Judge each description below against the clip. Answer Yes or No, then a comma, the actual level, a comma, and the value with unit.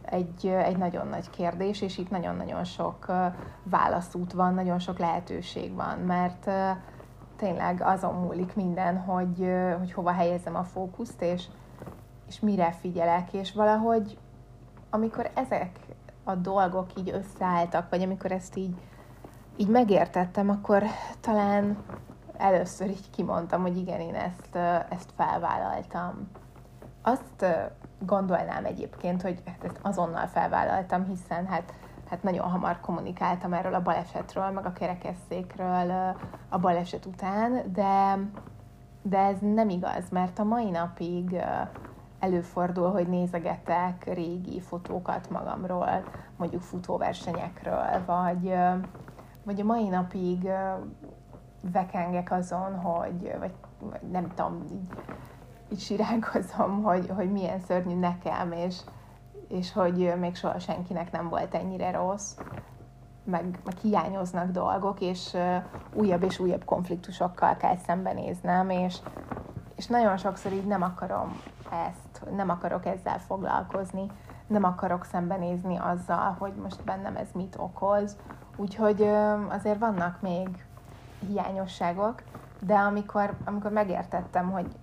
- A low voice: No, medium, 185 Hz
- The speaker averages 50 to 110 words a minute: No, average, 120 wpm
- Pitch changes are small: Yes, narrow, 1.9 semitones